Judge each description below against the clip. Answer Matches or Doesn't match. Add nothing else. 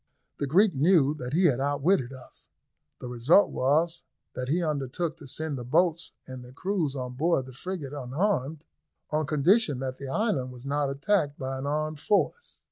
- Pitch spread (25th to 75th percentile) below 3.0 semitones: Doesn't match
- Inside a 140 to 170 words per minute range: Doesn't match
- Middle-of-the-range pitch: Matches